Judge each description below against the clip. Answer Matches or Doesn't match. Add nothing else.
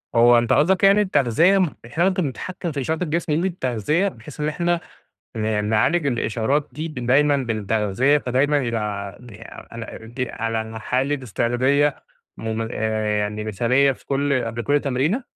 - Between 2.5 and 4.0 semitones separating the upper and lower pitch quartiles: Doesn't match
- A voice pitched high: Doesn't match